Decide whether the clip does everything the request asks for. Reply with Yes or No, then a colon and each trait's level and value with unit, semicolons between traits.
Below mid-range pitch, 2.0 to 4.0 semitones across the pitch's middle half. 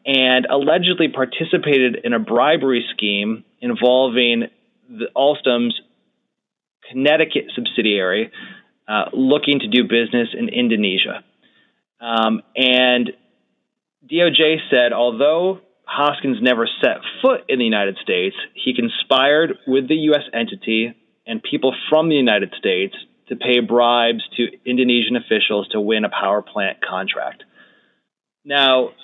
No: low, 130 Hz; average, 4.9 semitones